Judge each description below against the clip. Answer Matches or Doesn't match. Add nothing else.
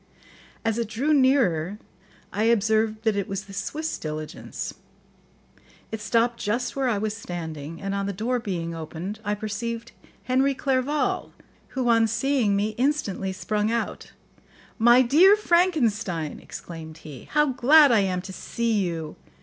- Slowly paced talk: Doesn't match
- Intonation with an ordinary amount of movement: Matches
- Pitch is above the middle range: Matches